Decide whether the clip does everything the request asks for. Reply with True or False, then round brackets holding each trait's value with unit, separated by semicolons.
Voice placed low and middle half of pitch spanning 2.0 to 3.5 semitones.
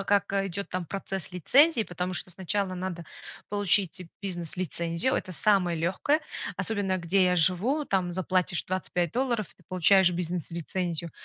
False (185 Hz; 2.4 semitones)